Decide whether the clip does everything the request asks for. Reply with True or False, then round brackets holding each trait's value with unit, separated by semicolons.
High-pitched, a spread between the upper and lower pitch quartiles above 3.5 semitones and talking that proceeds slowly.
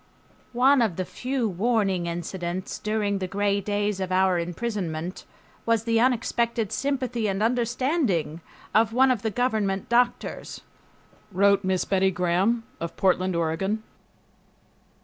True (205 Hz; 4.1 semitones; 130 wpm)